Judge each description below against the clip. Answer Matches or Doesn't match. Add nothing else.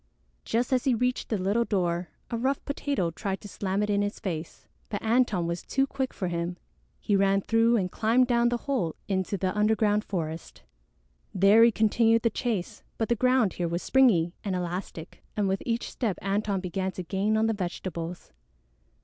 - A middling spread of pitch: Matches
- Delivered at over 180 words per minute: Matches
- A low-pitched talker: Doesn't match